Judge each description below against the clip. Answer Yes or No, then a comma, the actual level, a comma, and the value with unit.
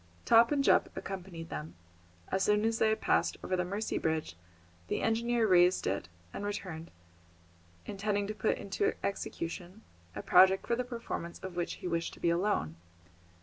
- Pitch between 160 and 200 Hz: Yes, high, 190 Hz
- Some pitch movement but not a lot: Yes, average, 3.9 semitones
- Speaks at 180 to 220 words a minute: No, average, 170 wpm